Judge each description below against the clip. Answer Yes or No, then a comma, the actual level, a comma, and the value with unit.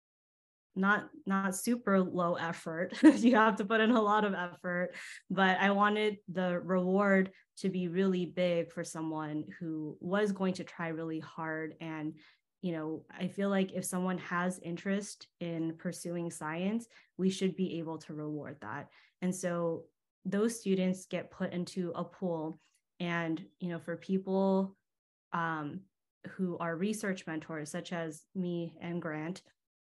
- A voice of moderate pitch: Yes, medium, 180 Hz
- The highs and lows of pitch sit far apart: No, narrow, 2.6 semitones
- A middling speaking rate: Yes, average, 150 wpm